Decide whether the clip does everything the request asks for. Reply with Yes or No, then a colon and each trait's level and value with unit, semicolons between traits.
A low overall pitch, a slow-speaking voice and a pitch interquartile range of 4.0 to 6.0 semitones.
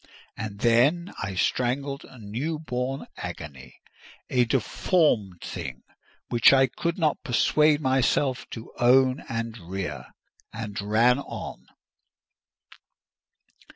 Yes: low, 125 Hz; slow, 95 wpm; average, 4.7 semitones